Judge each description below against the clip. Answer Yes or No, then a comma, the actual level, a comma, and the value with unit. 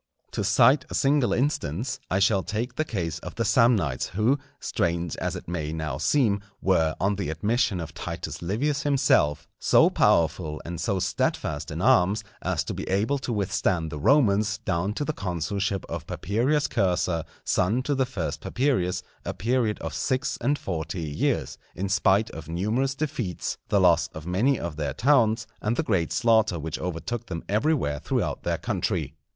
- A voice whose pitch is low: Yes, low, 100 Hz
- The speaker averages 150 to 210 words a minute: Yes, average, 175 wpm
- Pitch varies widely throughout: Yes, wide, 6.4 semitones